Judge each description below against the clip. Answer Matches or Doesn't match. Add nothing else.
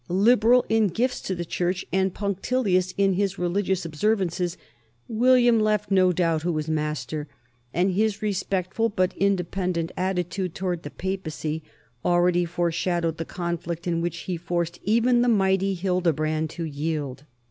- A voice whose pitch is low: Doesn't match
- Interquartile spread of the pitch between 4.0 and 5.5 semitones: Doesn't match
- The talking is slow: Doesn't match